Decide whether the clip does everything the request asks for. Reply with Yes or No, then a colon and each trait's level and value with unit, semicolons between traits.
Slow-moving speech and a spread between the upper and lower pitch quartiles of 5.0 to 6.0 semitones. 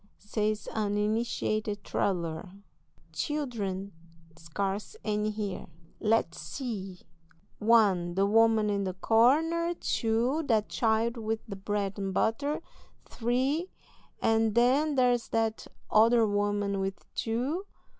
No: slow, 110 wpm; average, 3.0 semitones